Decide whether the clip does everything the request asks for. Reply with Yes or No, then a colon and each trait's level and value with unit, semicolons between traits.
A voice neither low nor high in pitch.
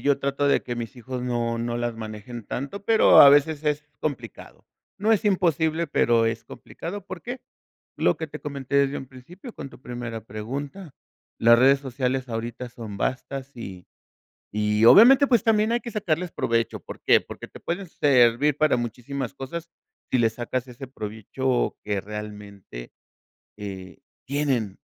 No: low, 130 Hz